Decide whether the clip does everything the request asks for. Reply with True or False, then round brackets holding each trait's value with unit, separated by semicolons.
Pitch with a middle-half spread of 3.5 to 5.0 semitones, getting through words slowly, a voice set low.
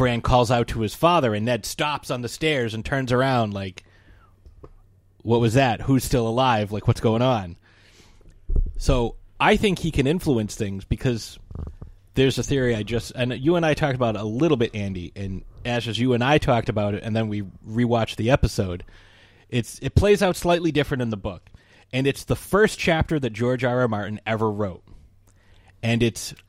False (4.7 semitones; 195 wpm; 115 Hz)